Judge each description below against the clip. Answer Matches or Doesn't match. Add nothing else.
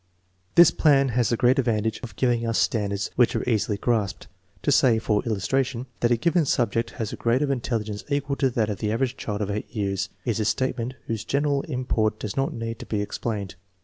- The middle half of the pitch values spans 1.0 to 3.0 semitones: Doesn't match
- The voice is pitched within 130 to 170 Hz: Doesn't match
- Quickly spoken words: Matches